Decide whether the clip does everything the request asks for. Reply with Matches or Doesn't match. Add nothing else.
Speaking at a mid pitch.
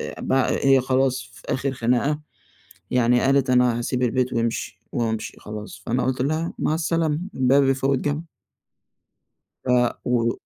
Doesn't match